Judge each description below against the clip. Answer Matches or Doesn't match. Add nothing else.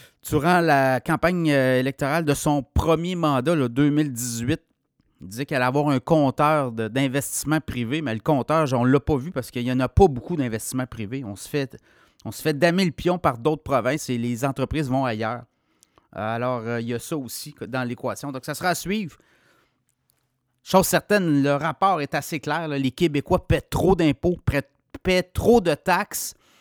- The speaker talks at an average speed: Matches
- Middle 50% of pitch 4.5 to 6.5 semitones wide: Doesn't match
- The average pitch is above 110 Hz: Matches